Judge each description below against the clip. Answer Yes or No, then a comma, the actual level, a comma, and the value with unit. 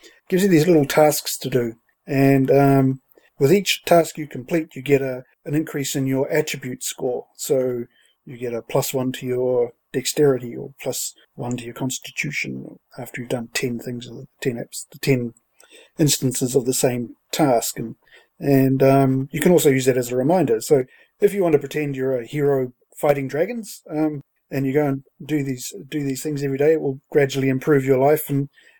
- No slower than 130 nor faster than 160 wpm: No, average, 195 wpm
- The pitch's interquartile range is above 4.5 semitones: No, average, 2.8 semitones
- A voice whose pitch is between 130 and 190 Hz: Yes, low, 135 Hz